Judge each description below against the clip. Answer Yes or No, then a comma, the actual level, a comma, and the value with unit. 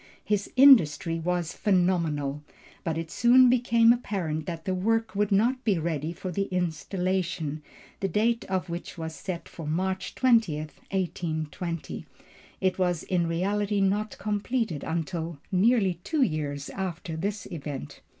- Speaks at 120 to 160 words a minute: Yes, average, 140 wpm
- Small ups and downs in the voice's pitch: No, average, 4.1 semitones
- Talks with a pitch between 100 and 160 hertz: No, medium, 185 Hz